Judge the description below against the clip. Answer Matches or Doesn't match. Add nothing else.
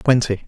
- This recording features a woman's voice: Doesn't match